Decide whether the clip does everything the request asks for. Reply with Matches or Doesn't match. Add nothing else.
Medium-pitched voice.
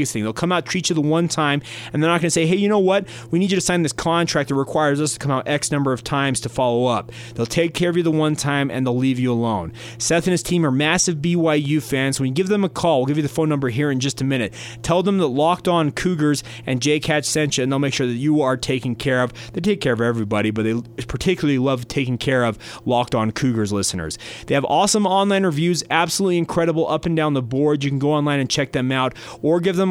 Matches